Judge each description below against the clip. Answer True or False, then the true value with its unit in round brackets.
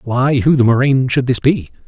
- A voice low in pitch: True (130 Hz)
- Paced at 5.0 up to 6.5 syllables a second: False (4.7 syllables/s)